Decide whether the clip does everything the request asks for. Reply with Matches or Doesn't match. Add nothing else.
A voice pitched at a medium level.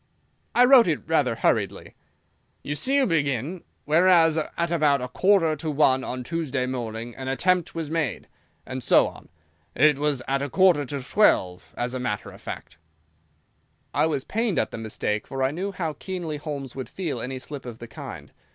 Matches